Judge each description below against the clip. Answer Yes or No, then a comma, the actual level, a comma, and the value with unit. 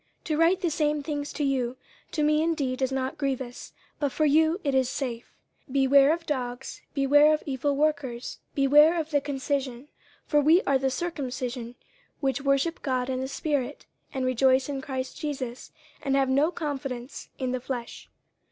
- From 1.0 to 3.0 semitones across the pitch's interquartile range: Yes, narrow, 2.5 semitones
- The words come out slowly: No, average, 180 wpm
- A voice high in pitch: Yes, very high, 275 Hz